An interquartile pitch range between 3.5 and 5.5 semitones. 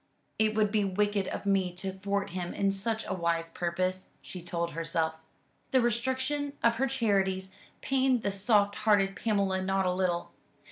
No: average, 2.9 semitones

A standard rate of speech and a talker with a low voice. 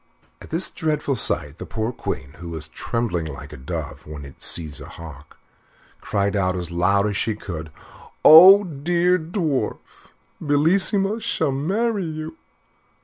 Yes: average, 150 wpm; low, 120 Hz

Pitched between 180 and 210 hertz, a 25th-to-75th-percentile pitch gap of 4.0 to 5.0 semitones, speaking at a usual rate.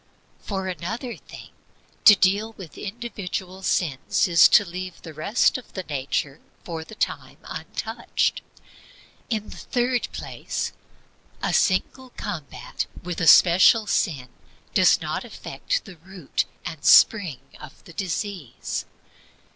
No: medium, 185 Hz; average, 4.4 semitones; slow, 125 wpm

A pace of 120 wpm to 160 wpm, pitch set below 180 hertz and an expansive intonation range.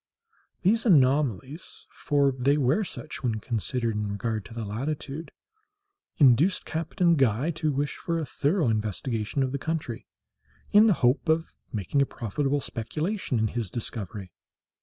Yes: average, 140 wpm; medium, 140 Hz; wide, 6.0 semitones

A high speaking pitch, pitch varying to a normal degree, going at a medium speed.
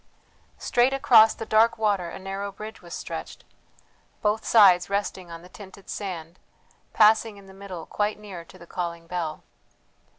Yes: high, 200 Hz; average, 3.5 semitones; average, 160 wpm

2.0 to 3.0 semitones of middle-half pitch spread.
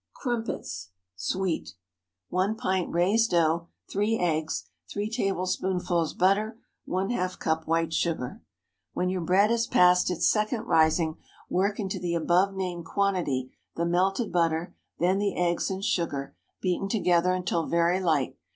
Yes: average, 2.7 semitones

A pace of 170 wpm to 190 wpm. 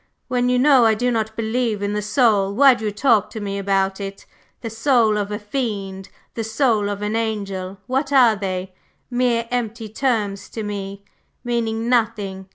Yes: average, 180 wpm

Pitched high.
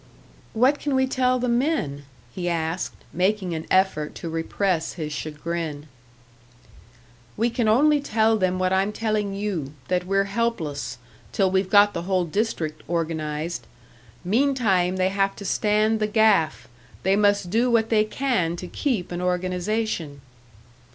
Yes: high, 195 Hz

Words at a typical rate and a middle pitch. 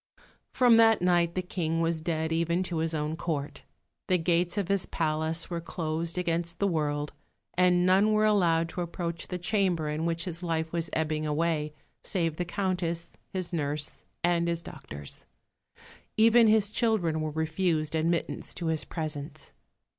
Yes: average, 160 wpm; medium, 170 Hz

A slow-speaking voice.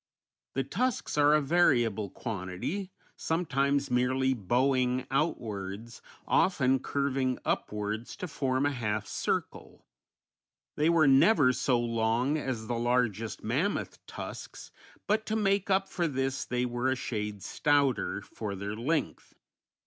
Yes: slow, 125 wpm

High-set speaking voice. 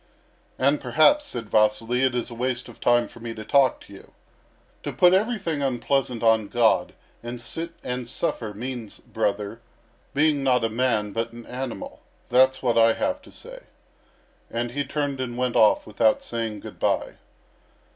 No: low, 125 Hz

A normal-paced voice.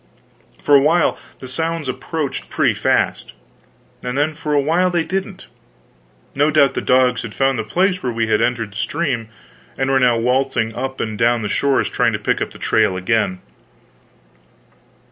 Yes: average, 180 wpm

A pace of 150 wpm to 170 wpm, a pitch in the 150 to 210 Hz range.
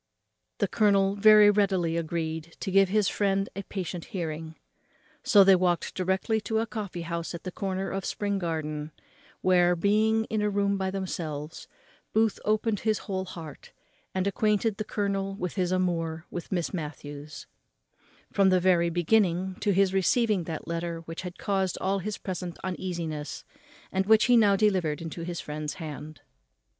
Yes: average, 165 wpm; medium, 185 Hz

